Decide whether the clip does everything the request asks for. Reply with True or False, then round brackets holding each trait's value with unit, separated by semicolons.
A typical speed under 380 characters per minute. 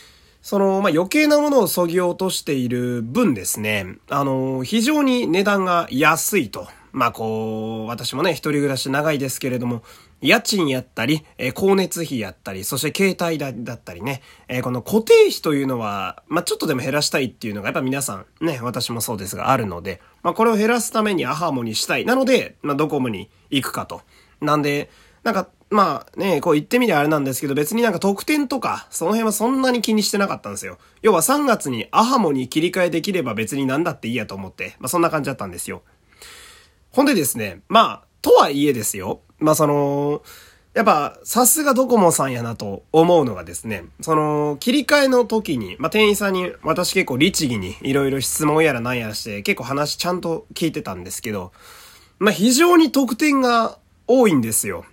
False (395 characters per minute)